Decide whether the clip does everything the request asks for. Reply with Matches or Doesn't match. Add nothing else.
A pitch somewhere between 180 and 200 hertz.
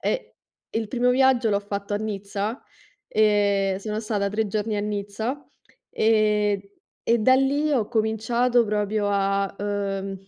Doesn't match